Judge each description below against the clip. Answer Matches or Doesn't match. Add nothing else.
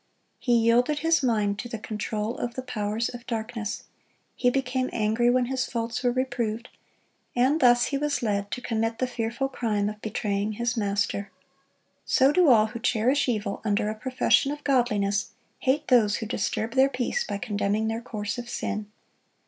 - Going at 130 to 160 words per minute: Doesn't match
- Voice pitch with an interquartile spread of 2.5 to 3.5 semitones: Matches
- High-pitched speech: Matches